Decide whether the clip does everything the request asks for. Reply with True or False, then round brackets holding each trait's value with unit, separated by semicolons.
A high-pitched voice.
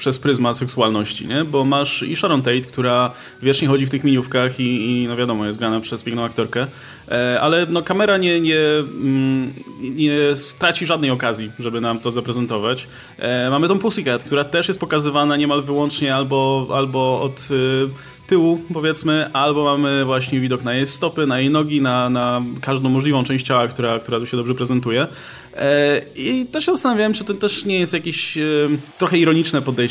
False (135 Hz)